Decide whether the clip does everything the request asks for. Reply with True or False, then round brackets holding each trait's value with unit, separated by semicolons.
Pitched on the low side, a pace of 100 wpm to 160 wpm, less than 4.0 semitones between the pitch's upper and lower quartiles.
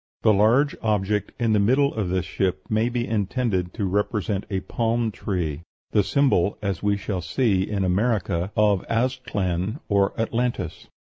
True (105 Hz; 155 wpm; 3.3 semitones)